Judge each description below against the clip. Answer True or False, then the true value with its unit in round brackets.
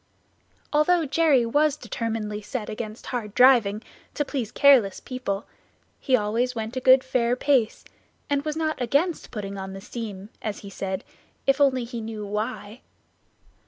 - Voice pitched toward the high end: True (240 Hz)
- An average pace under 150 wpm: False (155 wpm)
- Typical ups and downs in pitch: True (4.4 semitones)